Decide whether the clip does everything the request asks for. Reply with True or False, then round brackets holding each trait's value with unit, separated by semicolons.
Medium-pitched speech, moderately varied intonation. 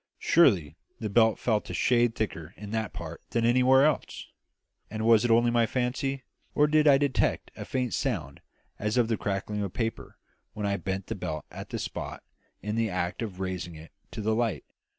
False (110 Hz; 3.7 semitones)